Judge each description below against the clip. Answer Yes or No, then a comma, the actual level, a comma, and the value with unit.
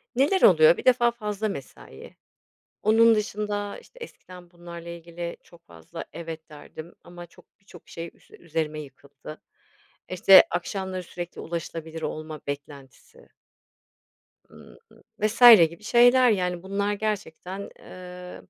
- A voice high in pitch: No, medium, 175 Hz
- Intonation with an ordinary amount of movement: Yes, average, 4.2 semitones